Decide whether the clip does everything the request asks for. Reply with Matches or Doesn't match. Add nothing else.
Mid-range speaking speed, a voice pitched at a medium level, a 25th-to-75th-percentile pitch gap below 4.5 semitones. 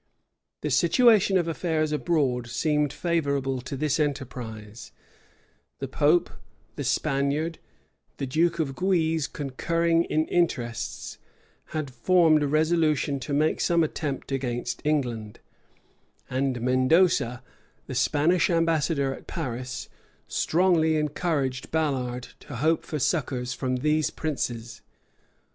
Doesn't match